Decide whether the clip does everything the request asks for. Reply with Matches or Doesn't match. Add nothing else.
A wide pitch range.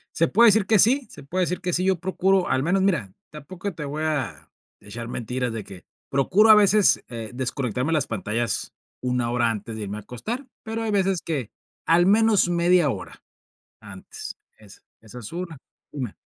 Matches